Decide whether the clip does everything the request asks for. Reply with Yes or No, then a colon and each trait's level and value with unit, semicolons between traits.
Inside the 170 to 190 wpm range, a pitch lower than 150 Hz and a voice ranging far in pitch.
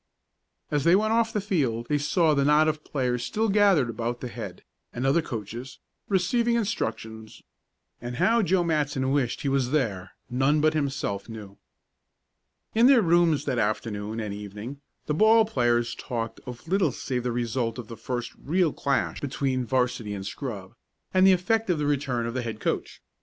Yes: average, 180 wpm; low, 135 Hz; wide, 6.2 semitones